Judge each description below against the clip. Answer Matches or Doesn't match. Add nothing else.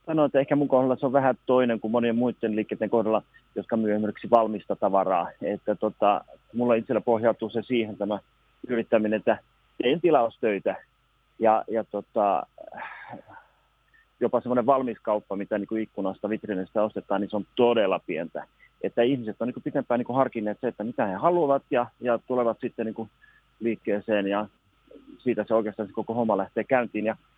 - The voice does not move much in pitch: Matches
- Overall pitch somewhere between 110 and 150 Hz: Matches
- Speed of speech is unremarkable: Doesn't match